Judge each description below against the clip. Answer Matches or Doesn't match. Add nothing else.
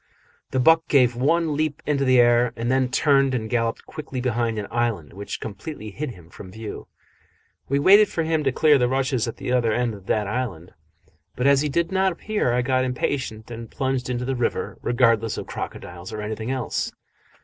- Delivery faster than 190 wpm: Matches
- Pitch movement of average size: Matches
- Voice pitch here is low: Matches